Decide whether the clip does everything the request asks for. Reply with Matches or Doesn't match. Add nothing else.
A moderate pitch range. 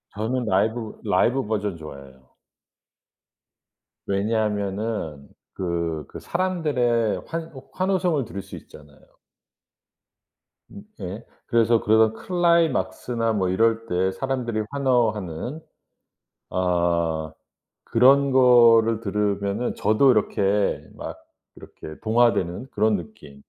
Matches